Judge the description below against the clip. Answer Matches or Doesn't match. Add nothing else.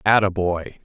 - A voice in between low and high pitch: Doesn't match